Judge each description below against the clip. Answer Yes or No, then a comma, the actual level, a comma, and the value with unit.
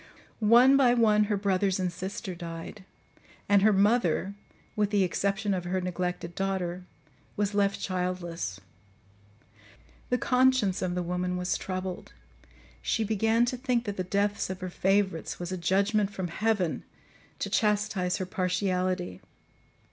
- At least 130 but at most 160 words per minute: Yes, average, 140 wpm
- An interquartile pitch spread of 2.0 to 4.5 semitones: Yes, narrow, 2.6 semitones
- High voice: Yes, high, 195 Hz